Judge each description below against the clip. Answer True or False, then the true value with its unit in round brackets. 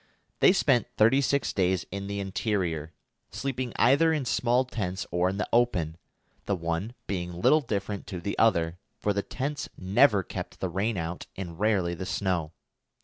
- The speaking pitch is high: False (100 Hz)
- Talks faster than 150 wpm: True (170 wpm)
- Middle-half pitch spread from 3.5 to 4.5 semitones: False (5.2 semitones)